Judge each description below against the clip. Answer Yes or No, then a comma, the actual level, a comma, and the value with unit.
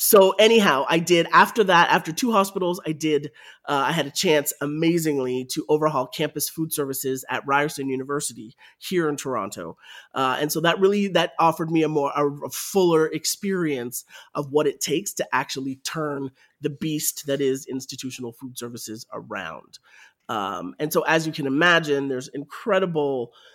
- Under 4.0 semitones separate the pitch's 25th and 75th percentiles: Yes, average, 3.6 semitones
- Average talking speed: Yes, average, 170 wpm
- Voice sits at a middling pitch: Yes, medium, 150 Hz